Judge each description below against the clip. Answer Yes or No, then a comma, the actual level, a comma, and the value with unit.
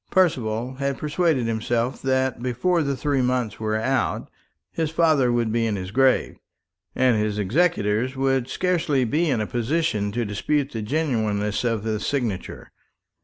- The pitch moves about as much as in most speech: Yes, average, 4.6 semitones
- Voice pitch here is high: No, low, 125 Hz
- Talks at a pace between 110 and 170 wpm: Yes, average, 155 wpm